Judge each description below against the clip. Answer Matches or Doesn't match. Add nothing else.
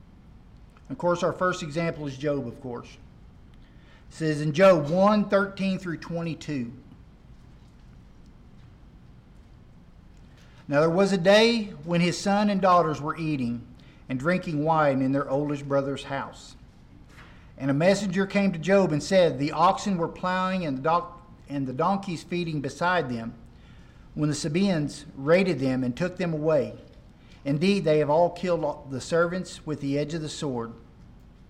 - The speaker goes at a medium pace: Matches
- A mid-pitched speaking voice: Matches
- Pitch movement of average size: Matches